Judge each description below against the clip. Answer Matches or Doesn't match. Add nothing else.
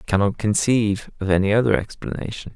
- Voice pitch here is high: Doesn't match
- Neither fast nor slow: Matches